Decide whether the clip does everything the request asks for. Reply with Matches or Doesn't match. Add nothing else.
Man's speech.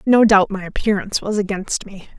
Doesn't match